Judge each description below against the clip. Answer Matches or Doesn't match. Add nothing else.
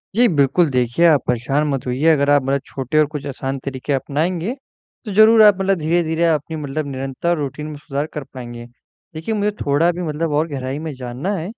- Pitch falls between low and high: Matches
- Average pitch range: Matches